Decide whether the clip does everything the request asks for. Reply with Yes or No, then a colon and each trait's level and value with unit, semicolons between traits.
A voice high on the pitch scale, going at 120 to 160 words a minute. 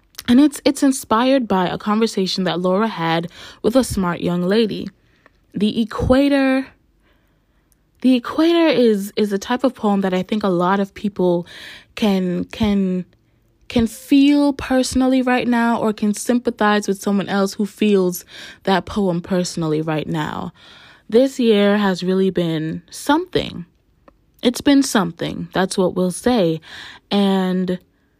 Yes: high, 205 Hz; average, 140 wpm